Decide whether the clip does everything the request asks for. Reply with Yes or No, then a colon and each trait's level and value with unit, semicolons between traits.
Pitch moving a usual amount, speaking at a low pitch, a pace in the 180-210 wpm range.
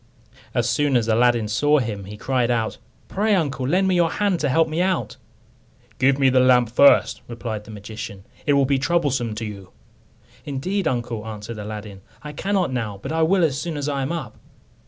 No: wide, 5.7 semitones; low, 130 Hz; average, 200 wpm